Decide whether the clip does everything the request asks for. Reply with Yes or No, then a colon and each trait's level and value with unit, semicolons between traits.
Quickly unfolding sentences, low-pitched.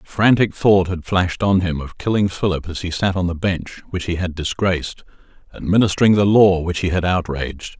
Yes: fast, 210 wpm; very low, 90 Hz